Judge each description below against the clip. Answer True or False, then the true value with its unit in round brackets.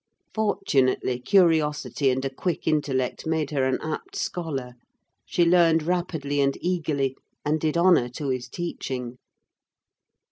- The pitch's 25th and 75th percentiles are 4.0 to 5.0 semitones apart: True (4.3 semitones)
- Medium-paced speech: False (130 wpm)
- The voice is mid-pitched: True (150 Hz)